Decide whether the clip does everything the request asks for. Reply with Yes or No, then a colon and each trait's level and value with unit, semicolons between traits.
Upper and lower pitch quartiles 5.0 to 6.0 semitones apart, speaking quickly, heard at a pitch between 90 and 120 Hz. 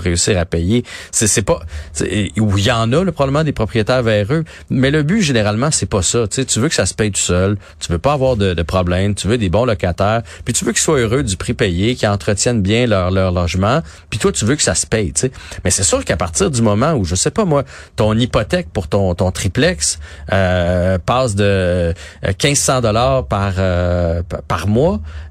Yes: wide, 5.4 semitones; fast, 230 wpm; low, 105 Hz